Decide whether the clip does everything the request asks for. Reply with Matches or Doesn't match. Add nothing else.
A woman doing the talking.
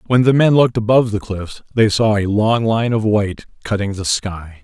Doesn't match